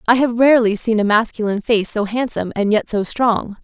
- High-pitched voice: Yes, high, 225 Hz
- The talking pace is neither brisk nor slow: No, fast, 215 wpm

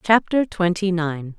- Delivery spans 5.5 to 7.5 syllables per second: No, 3.9 syllables/s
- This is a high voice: No, medium, 180 Hz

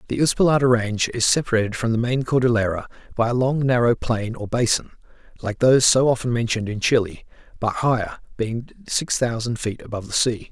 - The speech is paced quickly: No, average, 185 wpm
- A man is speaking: Yes, male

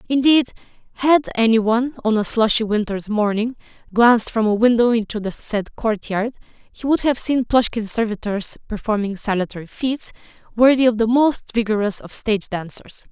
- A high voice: Yes, high, 225 Hz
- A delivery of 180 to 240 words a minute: No, average, 155 wpm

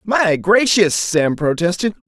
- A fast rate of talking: No, slow, 115 wpm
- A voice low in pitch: No, high, 190 Hz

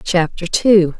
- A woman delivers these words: Yes, female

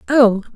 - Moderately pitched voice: No, high, 235 Hz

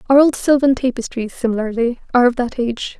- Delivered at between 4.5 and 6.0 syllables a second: No, 6.4 syllables/s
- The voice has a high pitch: Yes, high, 245 Hz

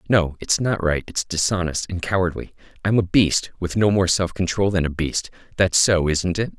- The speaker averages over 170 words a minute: Yes, average, 200 wpm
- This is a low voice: Yes, very low, 90 Hz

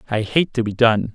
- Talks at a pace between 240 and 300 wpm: Yes, fast, 260 wpm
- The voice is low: Yes, low, 115 Hz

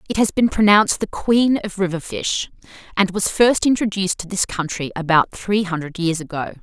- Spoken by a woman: Yes, female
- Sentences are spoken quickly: No, average, 190 wpm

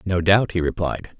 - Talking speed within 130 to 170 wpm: No, average, 200 wpm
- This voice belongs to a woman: No, male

